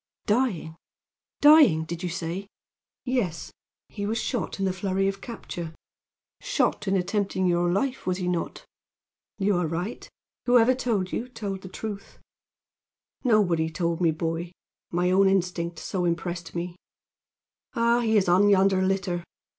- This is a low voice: No, high, 190 Hz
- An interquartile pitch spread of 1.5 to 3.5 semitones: Yes, average, 3.2 semitones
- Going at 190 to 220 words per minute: No, average, 145 wpm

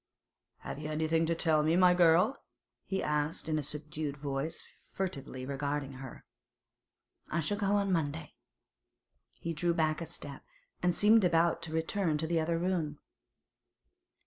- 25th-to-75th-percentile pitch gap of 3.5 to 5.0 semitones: No, narrow, 2.6 semitones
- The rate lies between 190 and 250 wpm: No, average, 150 wpm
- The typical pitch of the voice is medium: Yes, medium, 160 Hz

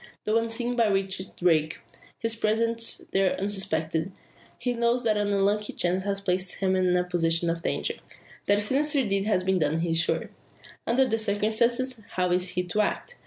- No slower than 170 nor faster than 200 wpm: Yes, average, 185 wpm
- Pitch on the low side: No, high, 200 Hz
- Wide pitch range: No, average, 4.0 semitones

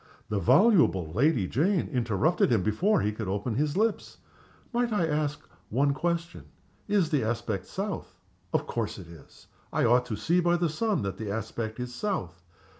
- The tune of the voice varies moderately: No, wide, 8.1 semitones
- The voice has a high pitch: No, low, 130 Hz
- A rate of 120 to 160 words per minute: No, average, 175 wpm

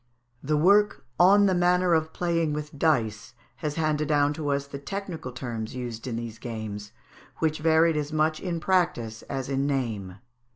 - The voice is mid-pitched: Yes, medium, 150 Hz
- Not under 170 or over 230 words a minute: Yes, average, 175 wpm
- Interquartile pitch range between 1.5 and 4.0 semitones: No, average, 5.2 semitones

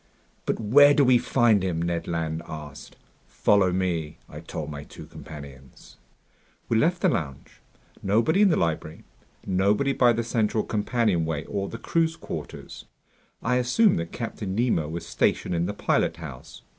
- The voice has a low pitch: Yes, very low, 95 Hz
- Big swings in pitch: Yes, wide, 6.7 semitones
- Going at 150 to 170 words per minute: Yes, average, 155 wpm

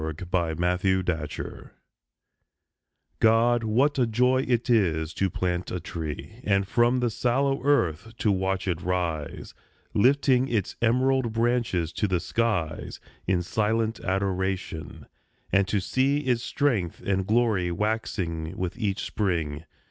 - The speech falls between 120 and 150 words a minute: Yes, slow, 135 wpm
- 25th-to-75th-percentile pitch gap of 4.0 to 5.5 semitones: Yes, average, 5.1 semitones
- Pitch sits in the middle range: No, low, 100 Hz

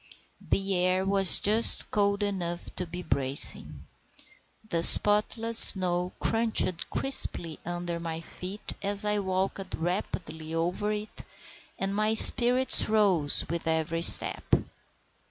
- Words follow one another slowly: Yes, slow, 120 wpm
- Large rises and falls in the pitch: No, average, 3.4 semitones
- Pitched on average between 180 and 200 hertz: Yes, high, 190 Hz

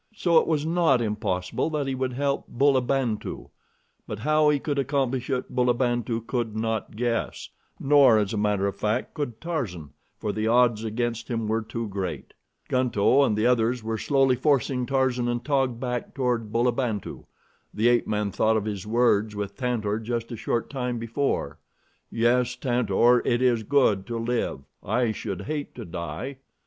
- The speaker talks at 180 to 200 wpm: No, average, 170 wpm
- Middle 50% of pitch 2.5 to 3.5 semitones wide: Yes, average, 3.2 semitones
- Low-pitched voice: Yes, low, 120 Hz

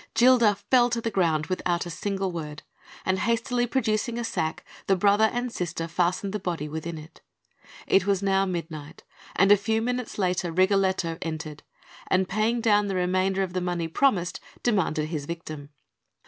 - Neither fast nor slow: Yes, average, 170 wpm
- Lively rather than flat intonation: No, average, 4.1 semitones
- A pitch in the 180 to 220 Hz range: Yes, high, 190 Hz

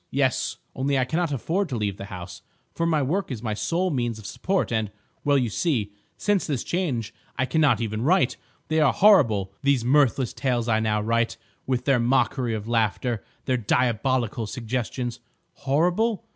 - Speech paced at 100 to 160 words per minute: No, average, 170 wpm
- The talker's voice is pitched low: Yes, low, 130 Hz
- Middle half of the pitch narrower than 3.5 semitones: No, average, 4.8 semitones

